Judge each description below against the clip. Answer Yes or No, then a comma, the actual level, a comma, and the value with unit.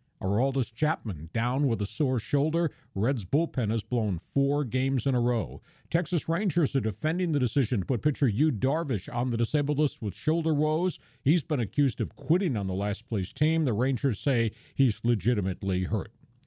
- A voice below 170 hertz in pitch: Yes, low, 135 Hz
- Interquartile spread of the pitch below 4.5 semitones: No, average, 5.0 semitones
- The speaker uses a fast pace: No, average, 180 wpm